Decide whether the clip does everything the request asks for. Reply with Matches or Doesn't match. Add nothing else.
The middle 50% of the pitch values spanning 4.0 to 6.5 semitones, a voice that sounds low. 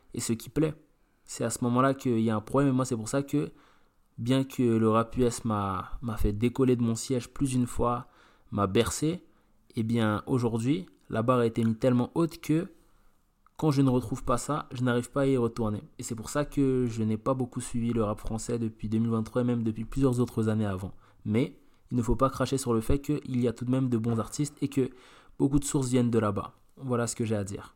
Doesn't match